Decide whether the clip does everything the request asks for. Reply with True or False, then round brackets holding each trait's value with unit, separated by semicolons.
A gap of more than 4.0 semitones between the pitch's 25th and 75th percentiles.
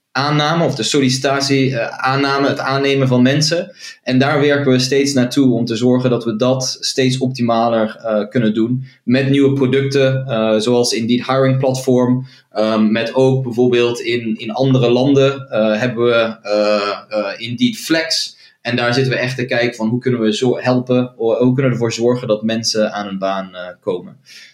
False (2.7 semitones)